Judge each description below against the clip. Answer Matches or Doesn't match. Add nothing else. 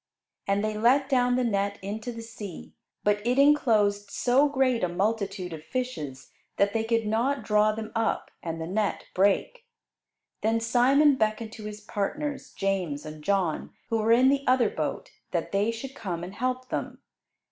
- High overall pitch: Matches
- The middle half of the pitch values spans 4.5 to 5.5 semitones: Doesn't match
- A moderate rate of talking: Matches